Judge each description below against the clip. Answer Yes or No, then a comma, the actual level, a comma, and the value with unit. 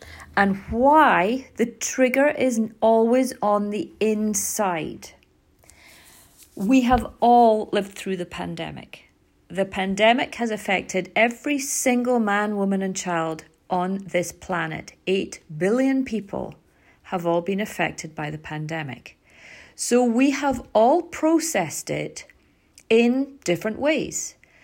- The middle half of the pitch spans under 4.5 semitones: No, wide, 5.4 semitones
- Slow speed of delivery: Yes, slow, 115 wpm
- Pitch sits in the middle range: No, high, 215 Hz